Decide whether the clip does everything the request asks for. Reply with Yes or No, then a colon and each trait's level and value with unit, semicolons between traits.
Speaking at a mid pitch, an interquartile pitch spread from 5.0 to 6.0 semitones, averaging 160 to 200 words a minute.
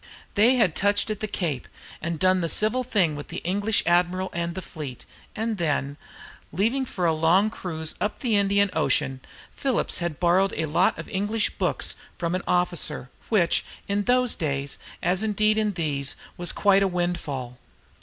No: medium, 180 Hz; average, 4.3 semitones; average, 175 wpm